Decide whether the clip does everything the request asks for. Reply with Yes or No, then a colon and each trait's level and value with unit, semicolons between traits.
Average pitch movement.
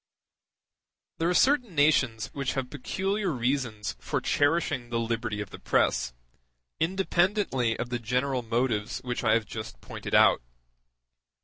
No: wide, 6.0 semitones